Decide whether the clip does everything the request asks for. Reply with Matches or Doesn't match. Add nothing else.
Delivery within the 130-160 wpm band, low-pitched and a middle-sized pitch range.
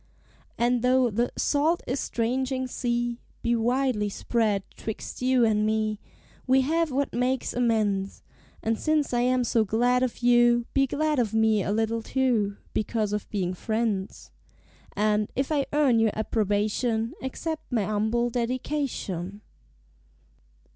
Doesn't match